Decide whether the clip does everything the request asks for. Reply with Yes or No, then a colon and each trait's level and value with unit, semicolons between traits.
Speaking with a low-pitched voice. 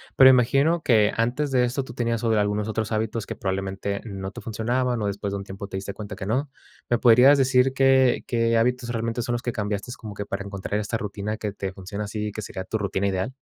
Yes: low, 110 Hz